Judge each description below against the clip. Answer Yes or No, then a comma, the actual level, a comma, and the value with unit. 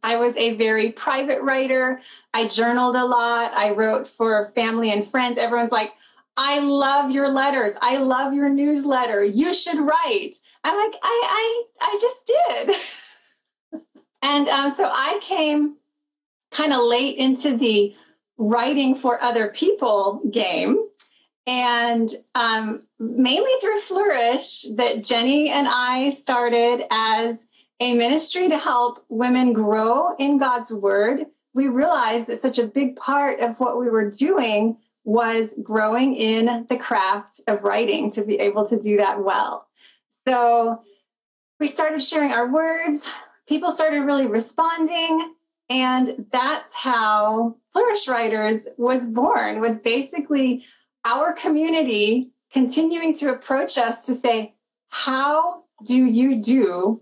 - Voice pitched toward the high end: Yes, very high, 255 Hz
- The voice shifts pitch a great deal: No, average, 4.3 semitones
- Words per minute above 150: No, slow, 135 wpm